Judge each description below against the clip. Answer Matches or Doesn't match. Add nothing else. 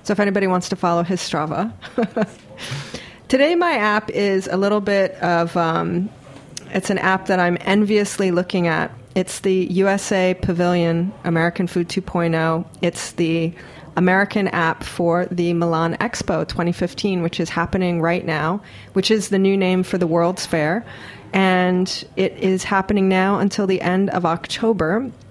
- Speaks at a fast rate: Doesn't match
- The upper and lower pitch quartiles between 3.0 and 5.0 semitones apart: Doesn't match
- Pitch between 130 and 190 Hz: Matches